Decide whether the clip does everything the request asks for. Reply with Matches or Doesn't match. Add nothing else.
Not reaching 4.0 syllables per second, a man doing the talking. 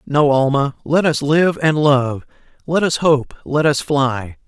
Matches